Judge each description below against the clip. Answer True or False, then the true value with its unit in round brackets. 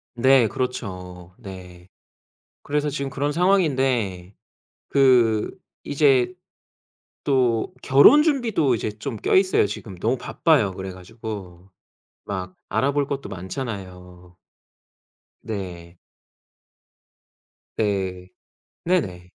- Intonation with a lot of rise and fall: True (6.9 semitones)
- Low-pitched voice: True (110 Hz)